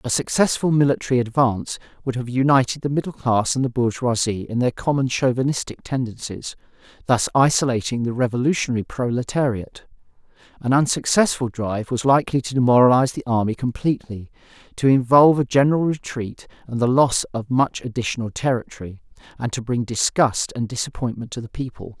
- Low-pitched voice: Yes, low, 125 Hz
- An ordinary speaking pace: Yes, average, 145 wpm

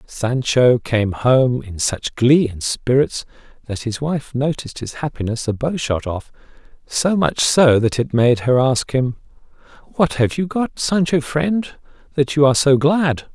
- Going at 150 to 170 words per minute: Yes, average, 165 wpm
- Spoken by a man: Yes, male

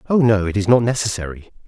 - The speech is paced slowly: No, fast, 215 wpm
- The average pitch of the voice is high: No, low, 110 Hz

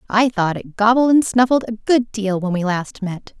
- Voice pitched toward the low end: No, high, 215 Hz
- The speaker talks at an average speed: No, fast, 230 wpm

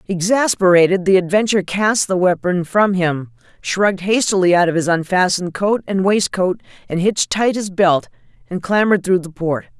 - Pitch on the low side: No, medium, 185 Hz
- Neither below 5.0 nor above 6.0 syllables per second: Yes, 5.1 syllables/s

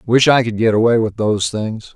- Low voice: Yes, low, 115 Hz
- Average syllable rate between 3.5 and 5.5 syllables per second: Yes, 5.2 syllables/s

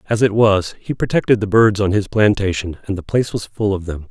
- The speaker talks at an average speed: No, fast, 250 wpm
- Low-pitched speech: Yes, low, 100 Hz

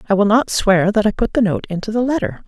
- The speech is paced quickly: Yes, fast, 290 wpm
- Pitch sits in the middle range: No, high, 210 Hz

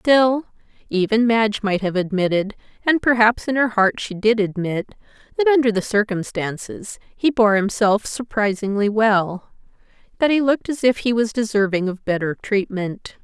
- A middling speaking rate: Yes, average, 155 wpm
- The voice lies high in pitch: Yes, high, 215 Hz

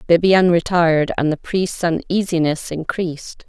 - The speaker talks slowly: Yes, slow, 120 wpm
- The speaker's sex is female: Yes, female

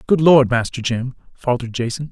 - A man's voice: Yes, male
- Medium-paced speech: Yes, average, 170 wpm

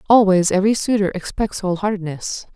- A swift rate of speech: No, average, 140 wpm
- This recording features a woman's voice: Yes, female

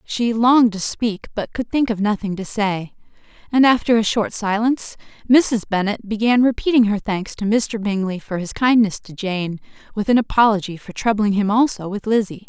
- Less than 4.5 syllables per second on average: No, 5.1 syllables/s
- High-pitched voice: Yes, high, 215 Hz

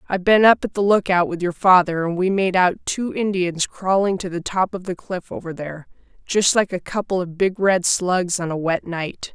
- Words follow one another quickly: Yes, fast, 230 wpm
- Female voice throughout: Yes, female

